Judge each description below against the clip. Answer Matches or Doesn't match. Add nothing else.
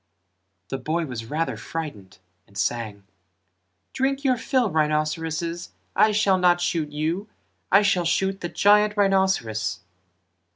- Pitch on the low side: Doesn't match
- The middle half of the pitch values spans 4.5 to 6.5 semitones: Matches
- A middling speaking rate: Doesn't match